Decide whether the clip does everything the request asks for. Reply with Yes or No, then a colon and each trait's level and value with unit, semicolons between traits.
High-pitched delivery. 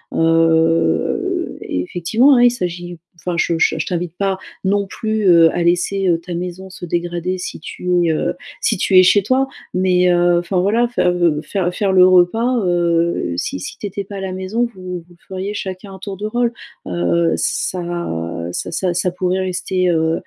No: medium, 180 Hz